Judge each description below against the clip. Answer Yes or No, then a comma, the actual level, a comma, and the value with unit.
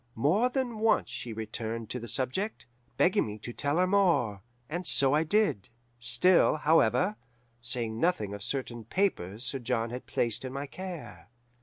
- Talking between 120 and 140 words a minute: No, average, 165 wpm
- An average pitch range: No, wide, 8.1 semitones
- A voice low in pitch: Yes, low, 130 Hz